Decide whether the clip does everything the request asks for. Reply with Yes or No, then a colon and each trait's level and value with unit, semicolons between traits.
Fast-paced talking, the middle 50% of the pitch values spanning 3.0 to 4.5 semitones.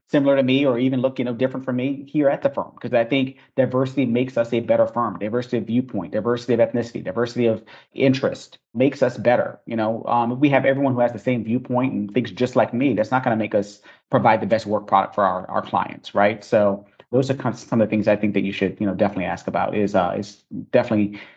Yes: fast, 255 wpm; average, 3.5 semitones